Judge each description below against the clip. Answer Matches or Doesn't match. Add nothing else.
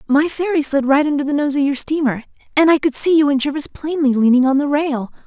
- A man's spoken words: Doesn't match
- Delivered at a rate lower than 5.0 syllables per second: Doesn't match